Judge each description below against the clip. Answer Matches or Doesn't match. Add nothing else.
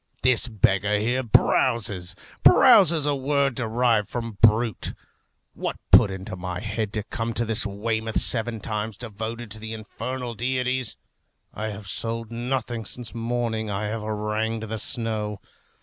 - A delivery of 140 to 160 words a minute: Matches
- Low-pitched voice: Matches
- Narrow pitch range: Matches